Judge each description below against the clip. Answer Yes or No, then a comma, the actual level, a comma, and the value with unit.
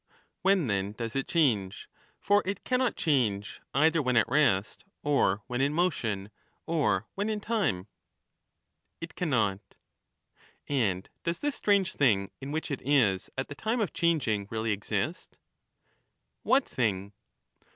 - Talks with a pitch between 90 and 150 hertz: Yes, low, 135 Hz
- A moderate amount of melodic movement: No, wide, 8.5 semitones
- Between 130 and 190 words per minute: Yes, average, 140 wpm